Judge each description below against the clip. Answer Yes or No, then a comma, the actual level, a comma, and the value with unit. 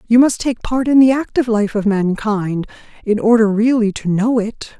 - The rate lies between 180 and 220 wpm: Yes, average, 200 wpm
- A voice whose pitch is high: Yes, high, 220 Hz